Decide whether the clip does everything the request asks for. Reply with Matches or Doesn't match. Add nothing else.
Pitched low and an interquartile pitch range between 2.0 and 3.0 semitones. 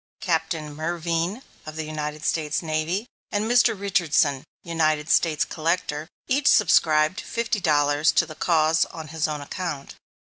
Doesn't match